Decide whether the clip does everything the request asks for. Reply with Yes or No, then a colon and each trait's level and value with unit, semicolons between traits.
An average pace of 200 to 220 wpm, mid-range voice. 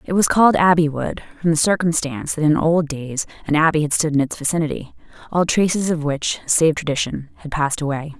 Yes: fast, 205 wpm; medium, 160 Hz